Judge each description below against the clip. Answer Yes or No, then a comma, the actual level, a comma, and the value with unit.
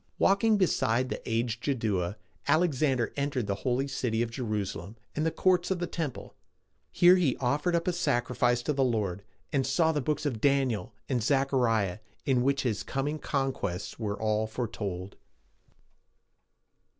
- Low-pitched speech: Yes, low, 130 Hz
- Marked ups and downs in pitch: No, average, 4.7 semitones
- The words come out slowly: No, average, 160 wpm